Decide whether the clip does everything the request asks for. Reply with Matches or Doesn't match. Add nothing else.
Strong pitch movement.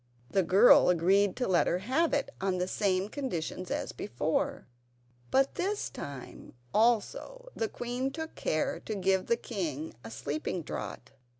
Matches